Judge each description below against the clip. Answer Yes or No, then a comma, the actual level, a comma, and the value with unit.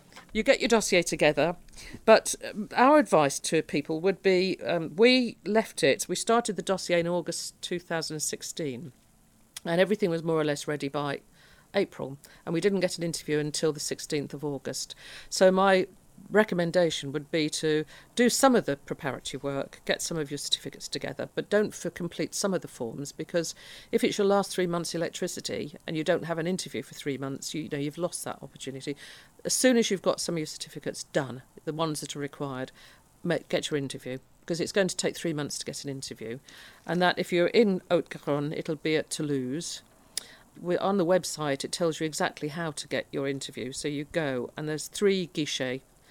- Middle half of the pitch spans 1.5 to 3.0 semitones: No, average, 4.0 semitones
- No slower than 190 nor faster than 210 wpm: Yes, average, 200 wpm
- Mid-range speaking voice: Yes, medium, 160 Hz